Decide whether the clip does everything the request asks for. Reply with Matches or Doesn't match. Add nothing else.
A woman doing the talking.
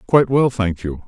Doesn't match